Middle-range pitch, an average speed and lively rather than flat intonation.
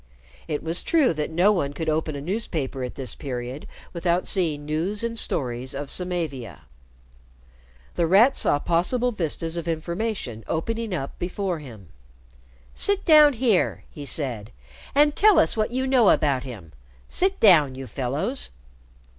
Yes: medium, 165 Hz; average, 150 wpm; wide, 7.5 semitones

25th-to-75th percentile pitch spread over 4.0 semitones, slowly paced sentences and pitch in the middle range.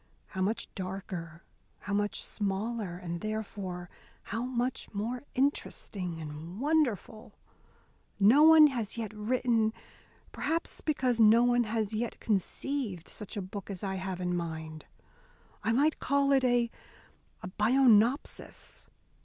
No: average, 4.6 semitones; slow, 125 wpm; high, 215 Hz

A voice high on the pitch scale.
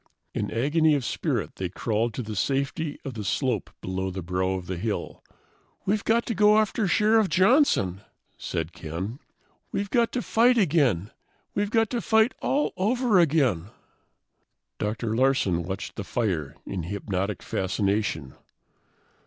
No: low, 120 Hz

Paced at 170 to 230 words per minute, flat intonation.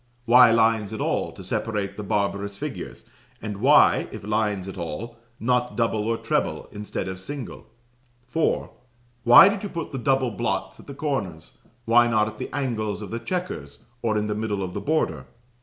No: average, 185 wpm; average, 3.5 semitones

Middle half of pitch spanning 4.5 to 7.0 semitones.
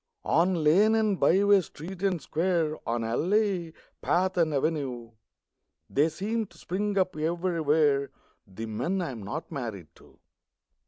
Yes: average, 5.2 semitones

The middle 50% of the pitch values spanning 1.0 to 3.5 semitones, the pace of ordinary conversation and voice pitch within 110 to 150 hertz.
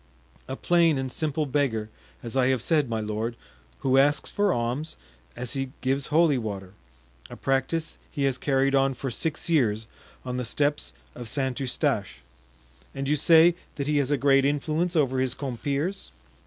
Yes: average, 2.9 semitones; average, 170 wpm; low, 135 Hz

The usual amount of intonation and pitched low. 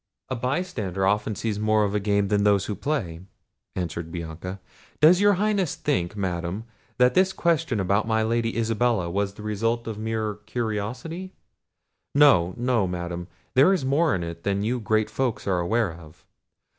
Yes: average, 4.7 semitones; low, 110 Hz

